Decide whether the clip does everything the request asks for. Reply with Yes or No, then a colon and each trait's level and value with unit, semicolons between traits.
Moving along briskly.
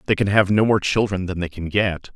Yes: fast, 280 wpm